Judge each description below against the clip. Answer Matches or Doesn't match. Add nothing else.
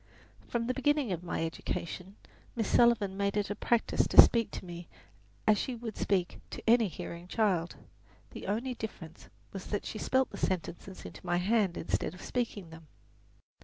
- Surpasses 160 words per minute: Matches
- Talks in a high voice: Matches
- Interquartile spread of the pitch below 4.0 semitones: Doesn't match